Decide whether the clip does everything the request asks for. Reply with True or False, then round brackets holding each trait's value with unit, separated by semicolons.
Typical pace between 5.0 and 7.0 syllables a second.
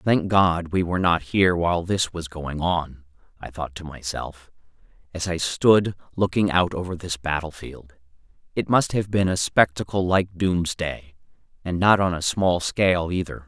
False (4.6 syllables/s)